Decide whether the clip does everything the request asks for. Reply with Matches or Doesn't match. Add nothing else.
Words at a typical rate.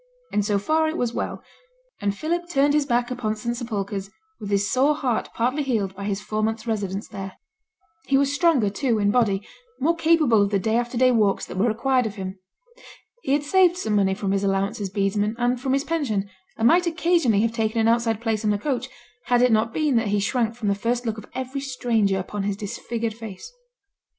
Doesn't match